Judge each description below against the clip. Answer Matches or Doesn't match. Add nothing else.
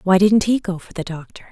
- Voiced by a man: Doesn't match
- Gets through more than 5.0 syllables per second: Matches